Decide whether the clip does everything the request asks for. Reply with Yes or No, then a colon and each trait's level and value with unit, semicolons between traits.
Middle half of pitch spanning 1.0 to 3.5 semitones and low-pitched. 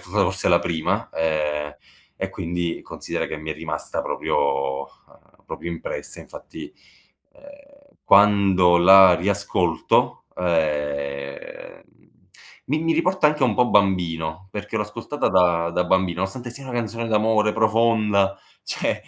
No: average, 5.3 semitones; very low, 95 Hz